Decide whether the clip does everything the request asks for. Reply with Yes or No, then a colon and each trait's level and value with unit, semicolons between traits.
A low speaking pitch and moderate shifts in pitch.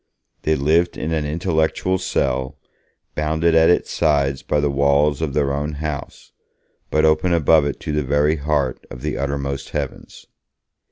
No: very low, 75 Hz; narrow, 2.0 semitones